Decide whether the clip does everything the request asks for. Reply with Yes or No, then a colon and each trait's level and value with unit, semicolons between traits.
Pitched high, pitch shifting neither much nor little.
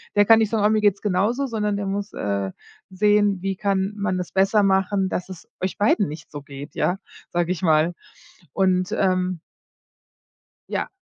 No: high, 195 Hz; narrow, 2.3 semitones